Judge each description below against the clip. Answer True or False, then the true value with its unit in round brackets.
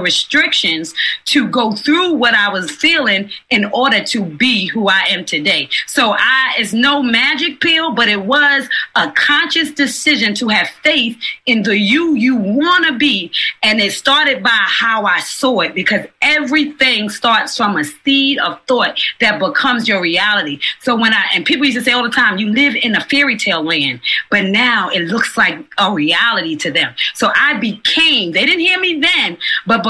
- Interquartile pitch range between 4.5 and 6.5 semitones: True (5.6 semitones)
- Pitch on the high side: True (245 Hz)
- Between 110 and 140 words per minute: False (190 wpm)